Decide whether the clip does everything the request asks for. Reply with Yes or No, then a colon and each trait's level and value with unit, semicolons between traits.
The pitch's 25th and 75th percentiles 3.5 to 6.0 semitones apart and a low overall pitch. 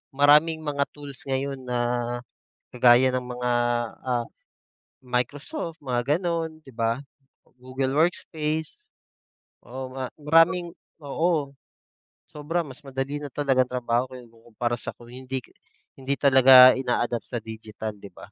No: average, 3.1 semitones; low, 130 Hz